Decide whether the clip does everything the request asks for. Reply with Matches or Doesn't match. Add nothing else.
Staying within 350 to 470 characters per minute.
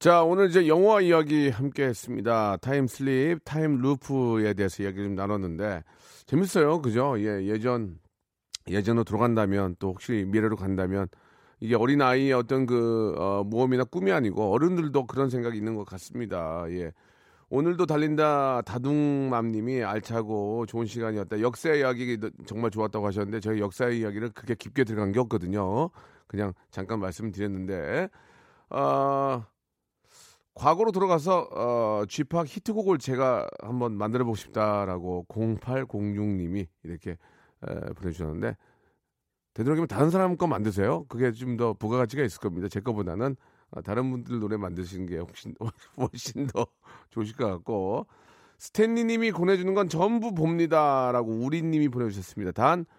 Doesn't match